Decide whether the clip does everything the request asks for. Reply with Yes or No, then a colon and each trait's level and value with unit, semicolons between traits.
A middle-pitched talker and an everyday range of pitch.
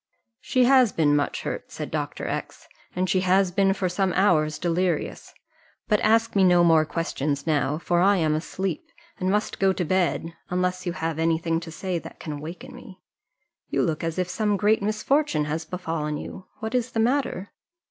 Yes: medium, 180 Hz; average, 3.7 semitones